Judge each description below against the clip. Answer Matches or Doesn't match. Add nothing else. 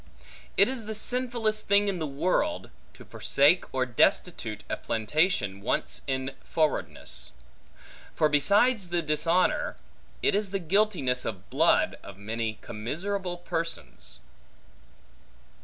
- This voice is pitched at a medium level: Matches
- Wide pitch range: Matches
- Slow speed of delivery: Matches